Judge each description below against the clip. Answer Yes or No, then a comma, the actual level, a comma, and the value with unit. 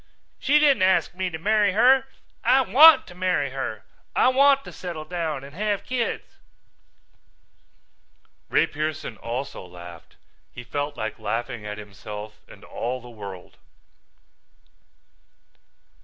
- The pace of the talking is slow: Yes, slow, 125 wpm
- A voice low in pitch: No, medium, 155 Hz